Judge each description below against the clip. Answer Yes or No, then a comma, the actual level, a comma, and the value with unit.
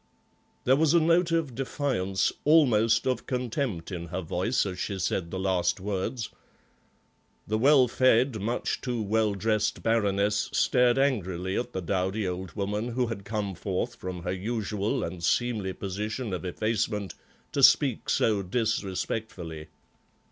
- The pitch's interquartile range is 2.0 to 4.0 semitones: No, average, 4.5 semitones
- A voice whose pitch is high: No, low, 105 Hz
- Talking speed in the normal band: Yes, average, 145 wpm